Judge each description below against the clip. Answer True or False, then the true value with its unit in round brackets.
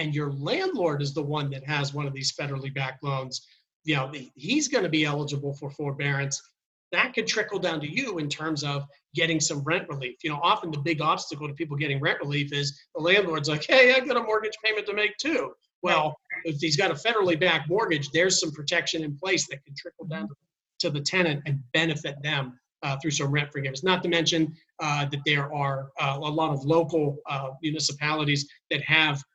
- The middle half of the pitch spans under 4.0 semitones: True (2.9 semitones)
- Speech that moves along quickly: True (215 wpm)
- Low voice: False (155 Hz)